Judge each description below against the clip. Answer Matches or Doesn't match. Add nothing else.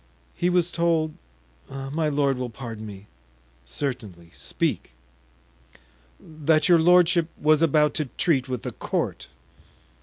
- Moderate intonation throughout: Doesn't match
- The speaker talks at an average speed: Doesn't match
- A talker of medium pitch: Matches